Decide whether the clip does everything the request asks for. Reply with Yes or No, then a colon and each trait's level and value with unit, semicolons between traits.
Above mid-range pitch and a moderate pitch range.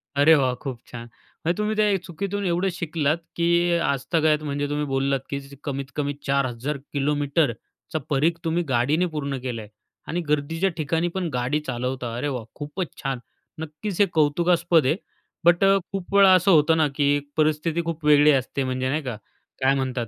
No: medium, 150 Hz; average, 3.8 semitones